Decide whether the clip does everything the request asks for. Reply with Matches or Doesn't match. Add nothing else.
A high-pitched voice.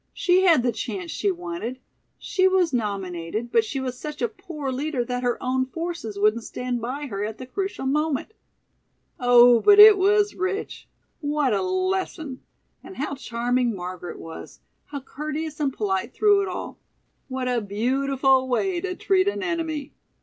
Matches